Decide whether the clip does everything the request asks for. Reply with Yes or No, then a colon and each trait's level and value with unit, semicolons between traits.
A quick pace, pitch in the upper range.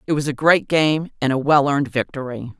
No: fast, 230 wpm; medium, 140 Hz